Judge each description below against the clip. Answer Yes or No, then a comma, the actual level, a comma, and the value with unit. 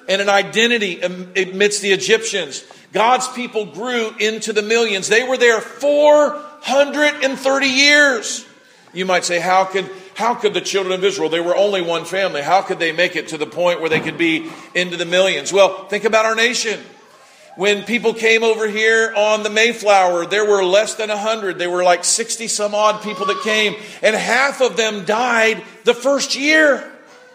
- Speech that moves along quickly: No, average, 180 wpm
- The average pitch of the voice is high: Yes, high, 210 Hz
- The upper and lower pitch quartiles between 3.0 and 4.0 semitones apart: Yes, average, 3.6 semitones